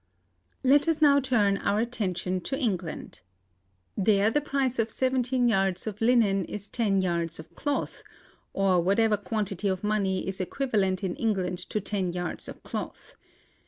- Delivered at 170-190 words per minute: No, average, 155 wpm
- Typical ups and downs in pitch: Yes, average, 4.3 semitones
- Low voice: No, high, 205 Hz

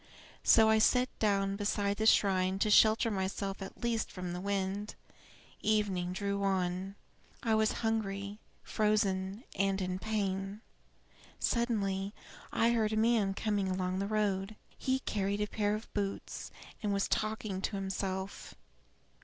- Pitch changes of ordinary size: No, narrow, 2.0 semitones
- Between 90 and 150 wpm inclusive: Yes, average, 140 wpm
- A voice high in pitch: Yes, high, 200 Hz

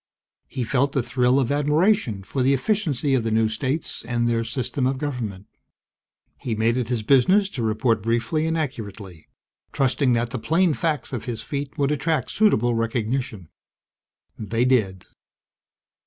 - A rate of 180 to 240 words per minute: No, average, 155 wpm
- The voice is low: Yes, low, 125 Hz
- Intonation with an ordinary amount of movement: Yes, average, 3.8 semitones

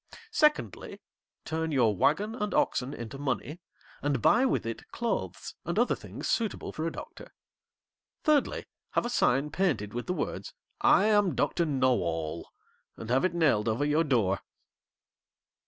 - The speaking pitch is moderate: Yes, medium, 145 Hz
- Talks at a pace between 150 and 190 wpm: Yes, average, 155 wpm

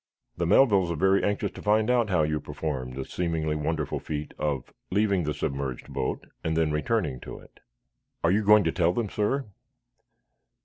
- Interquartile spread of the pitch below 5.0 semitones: No, average, 5.3 semitones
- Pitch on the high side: No, very low, 85 Hz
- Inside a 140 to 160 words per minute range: No, average, 180 wpm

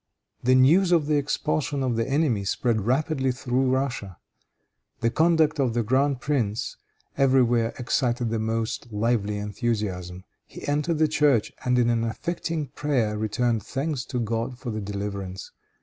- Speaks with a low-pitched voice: Yes, low, 120 Hz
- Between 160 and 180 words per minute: No, average, 150 wpm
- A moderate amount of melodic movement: Yes, average, 4.2 semitones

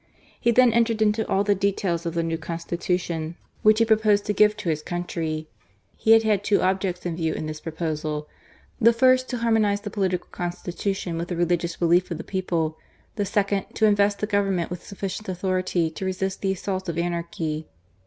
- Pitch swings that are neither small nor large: Yes, average, 3.6 semitones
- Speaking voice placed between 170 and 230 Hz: Yes, medium, 185 Hz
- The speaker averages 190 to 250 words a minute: Yes, average, 195 wpm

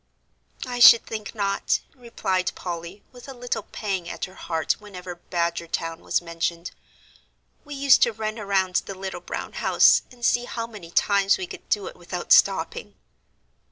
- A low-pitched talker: No, high, 200 Hz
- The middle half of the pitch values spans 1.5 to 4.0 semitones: No, average, 5.2 semitones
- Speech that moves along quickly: No, average, 160 wpm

